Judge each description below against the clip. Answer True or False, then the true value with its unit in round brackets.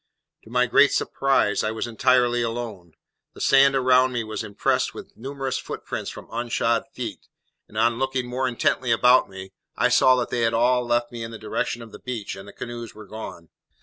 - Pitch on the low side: True (120 Hz)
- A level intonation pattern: True (2.3 semitones)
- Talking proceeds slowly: False (200 wpm)